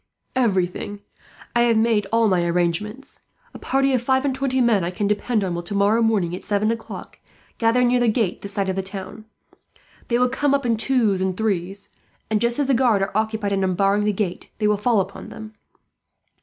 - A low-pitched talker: No, high, 215 Hz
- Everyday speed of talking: No, fast, 210 wpm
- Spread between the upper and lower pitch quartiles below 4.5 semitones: Yes, average, 3.5 semitones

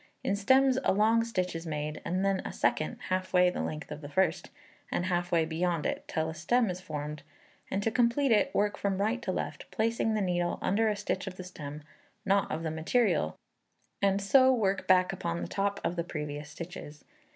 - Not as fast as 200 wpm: No, fast, 205 wpm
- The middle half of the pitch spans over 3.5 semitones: Yes, average, 4.2 semitones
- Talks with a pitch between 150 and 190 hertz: Yes, medium, 185 Hz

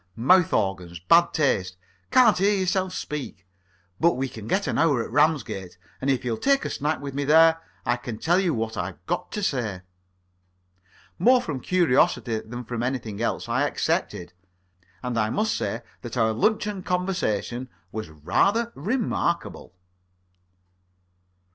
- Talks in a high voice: No, low, 135 Hz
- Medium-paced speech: Yes, average, 150 wpm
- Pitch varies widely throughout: Yes, wide, 8.4 semitones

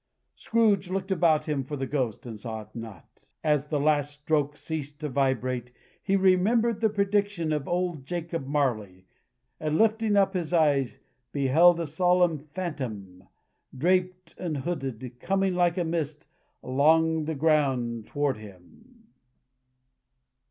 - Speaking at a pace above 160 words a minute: No, average, 140 wpm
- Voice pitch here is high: No, medium, 155 Hz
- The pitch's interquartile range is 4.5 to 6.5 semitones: Yes, average, 5.1 semitones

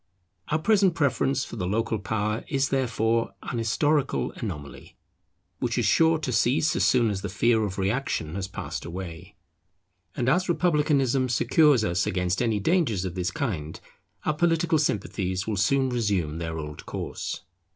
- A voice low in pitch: Yes, low, 115 Hz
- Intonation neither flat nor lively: No, wide, 6.7 semitones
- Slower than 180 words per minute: Yes, average, 160 wpm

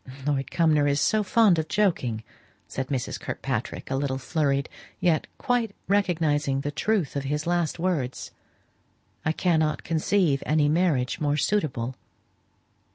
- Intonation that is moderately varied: Yes, average, 4.2 semitones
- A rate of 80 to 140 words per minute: Yes, slow, 135 wpm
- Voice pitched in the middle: Yes, medium, 155 Hz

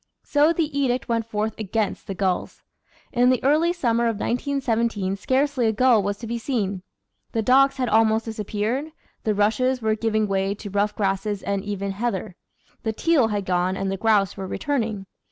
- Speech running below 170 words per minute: No, average, 180 wpm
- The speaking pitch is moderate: No, high, 220 Hz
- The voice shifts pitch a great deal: No, average, 3.8 semitones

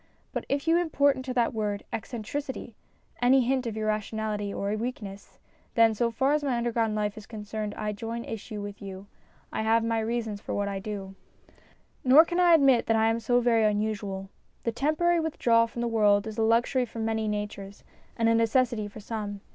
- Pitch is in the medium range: No, high, 225 Hz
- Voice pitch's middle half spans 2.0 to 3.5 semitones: Yes, average, 2.7 semitones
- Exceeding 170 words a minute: Yes, average, 195 wpm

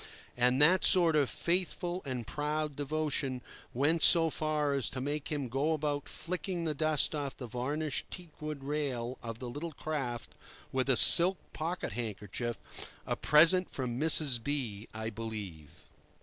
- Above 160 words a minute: No, average, 150 wpm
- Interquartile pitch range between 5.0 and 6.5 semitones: No, average, 4.1 semitones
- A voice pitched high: No, medium, 145 Hz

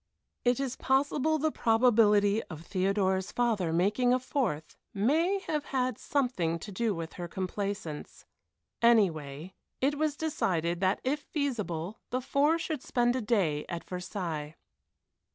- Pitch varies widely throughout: Yes, wide, 6.6 semitones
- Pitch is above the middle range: Yes, high, 215 Hz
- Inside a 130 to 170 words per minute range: Yes, average, 140 wpm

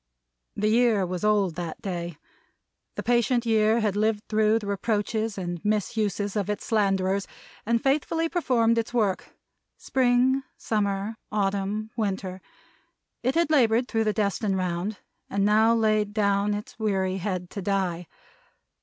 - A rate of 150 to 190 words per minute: No, average, 140 wpm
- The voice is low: No, high, 210 Hz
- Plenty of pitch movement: No, narrow, 2.5 semitones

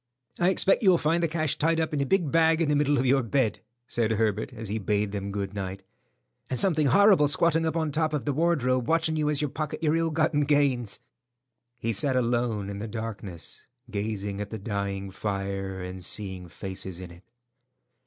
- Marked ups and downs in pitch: Yes, wide, 7.5 semitones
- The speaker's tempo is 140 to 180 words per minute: No, fast, 205 wpm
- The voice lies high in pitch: No, low, 125 Hz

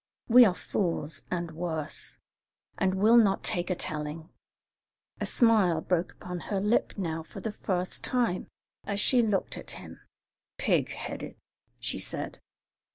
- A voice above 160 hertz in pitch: Yes, medium, 185 Hz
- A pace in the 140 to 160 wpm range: Yes, average, 145 wpm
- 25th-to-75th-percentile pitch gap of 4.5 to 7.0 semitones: No, average, 4.1 semitones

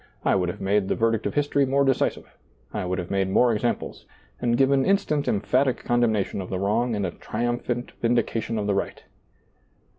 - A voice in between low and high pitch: No, low, 115 Hz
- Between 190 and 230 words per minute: Yes, fast, 205 wpm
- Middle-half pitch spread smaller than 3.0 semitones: No, average, 4.1 semitones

